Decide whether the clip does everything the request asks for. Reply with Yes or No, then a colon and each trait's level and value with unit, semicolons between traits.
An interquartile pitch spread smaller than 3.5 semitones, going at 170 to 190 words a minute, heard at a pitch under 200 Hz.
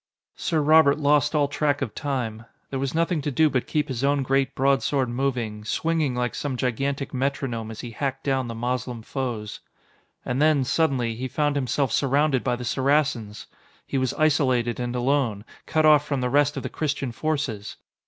Yes: average, 2.9 semitones; average, 185 wpm; low, 135 Hz